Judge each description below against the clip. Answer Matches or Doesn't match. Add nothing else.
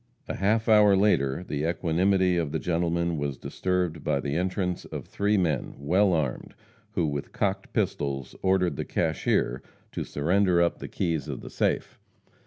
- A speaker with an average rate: Matches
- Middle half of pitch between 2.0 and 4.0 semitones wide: Doesn't match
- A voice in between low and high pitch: Doesn't match